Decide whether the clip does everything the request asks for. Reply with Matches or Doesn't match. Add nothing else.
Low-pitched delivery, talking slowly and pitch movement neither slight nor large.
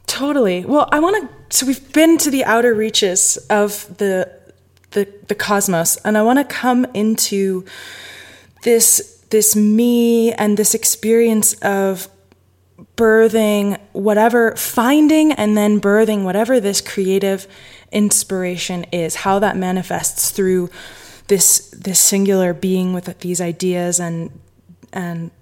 Doesn't match